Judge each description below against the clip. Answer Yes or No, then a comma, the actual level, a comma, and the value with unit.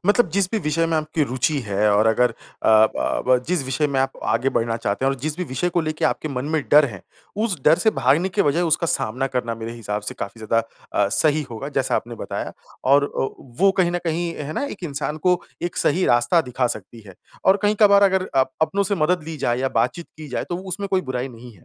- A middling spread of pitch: No, wide, 6.4 semitones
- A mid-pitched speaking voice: Yes, medium, 145 Hz